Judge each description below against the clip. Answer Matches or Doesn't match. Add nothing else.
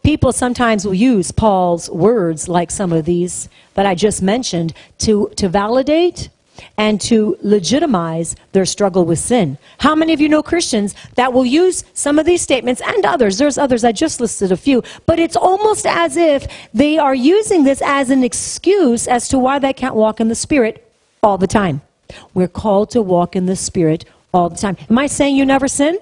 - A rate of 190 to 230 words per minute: Matches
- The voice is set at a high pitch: Matches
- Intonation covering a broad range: Matches